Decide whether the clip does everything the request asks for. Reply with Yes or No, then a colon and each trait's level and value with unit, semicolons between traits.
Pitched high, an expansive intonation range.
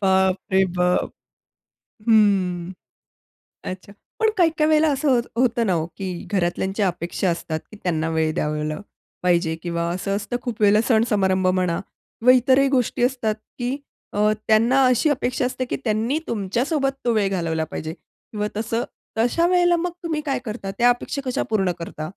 Yes: high, 210 Hz; wide, 5.8 semitones